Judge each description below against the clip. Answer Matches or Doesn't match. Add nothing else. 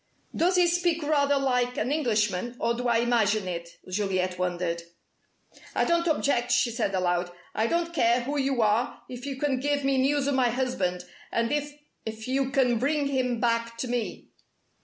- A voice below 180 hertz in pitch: Doesn't match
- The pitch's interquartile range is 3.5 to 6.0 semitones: Matches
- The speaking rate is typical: Matches